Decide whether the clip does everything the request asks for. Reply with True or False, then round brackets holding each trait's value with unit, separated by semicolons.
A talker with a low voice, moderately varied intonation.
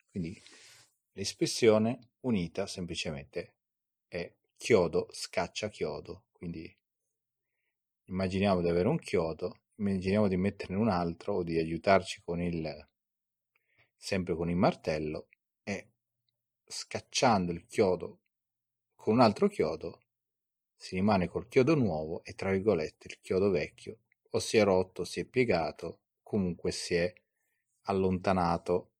True (95 Hz; 3.1 semitones)